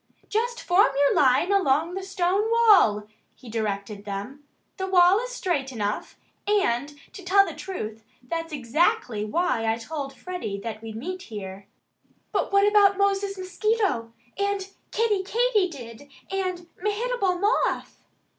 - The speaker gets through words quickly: No, slow, 135 wpm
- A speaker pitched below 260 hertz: No, very high, 355 Hz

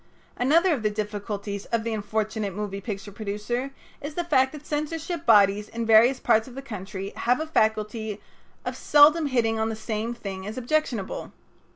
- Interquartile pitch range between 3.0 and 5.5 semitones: Yes, average, 4.2 semitones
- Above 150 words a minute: Yes, average, 175 wpm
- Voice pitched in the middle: No, high, 220 Hz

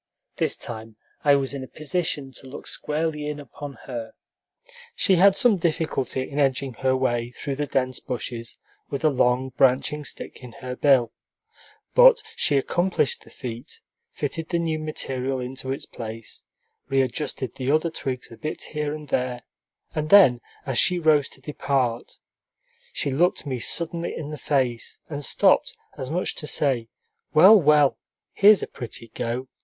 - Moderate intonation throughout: Yes, average, 3.4 semitones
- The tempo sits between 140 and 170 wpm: Yes, average, 165 wpm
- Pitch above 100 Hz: Yes, medium, 140 Hz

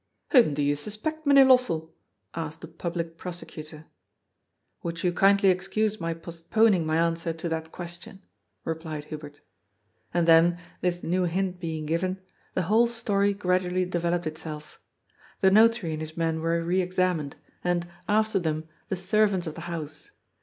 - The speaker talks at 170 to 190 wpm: No, average, 160 wpm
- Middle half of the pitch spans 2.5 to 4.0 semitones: Yes, average, 2.8 semitones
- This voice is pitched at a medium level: Yes, medium, 175 Hz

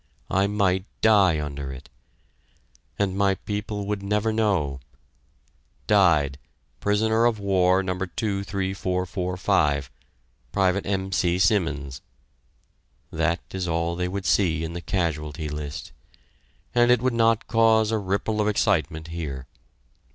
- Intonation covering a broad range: No, average, 3.9 semitones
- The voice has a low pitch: Yes, very low, 95 Hz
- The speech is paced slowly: Yes, slow, 120 wpm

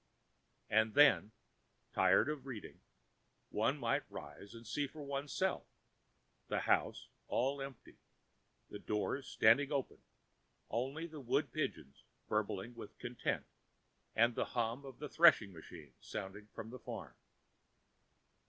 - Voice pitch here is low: Yes, low, 120 Hz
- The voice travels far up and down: No, average, 4.7 semitones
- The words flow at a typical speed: No, slow, 125 wpm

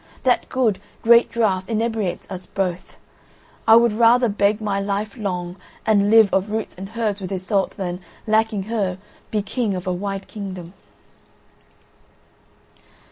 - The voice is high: Yes, high, 205 Hz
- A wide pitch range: No, average, 2.7 semitones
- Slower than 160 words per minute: Yes, average, 140 wpm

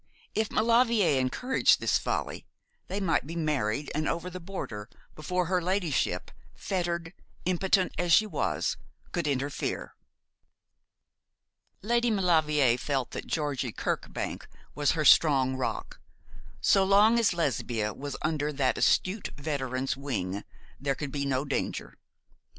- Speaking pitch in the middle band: Yes, medium, 155 Hz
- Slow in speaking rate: Yes, slow, 130 wpm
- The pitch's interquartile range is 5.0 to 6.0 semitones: Yes, average, 5.3 semitones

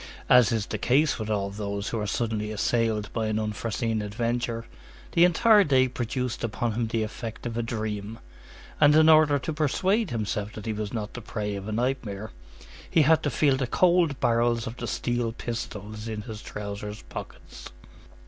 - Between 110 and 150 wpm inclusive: No, average, 185 wpm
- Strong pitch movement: No, average, 3.2 semitones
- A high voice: No, low, 115 Hz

